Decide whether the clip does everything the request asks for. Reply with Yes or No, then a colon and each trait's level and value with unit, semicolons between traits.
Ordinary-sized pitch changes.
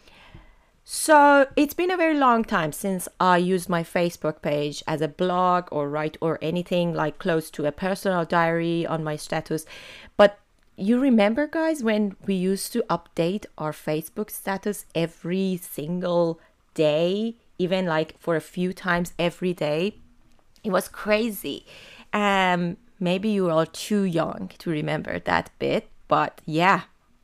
Yes: average, 4.0 semitones